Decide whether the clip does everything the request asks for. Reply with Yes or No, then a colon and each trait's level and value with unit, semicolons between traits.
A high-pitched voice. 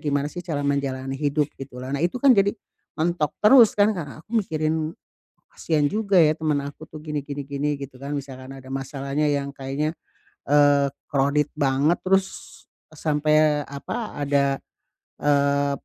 No: medium, 145 Hz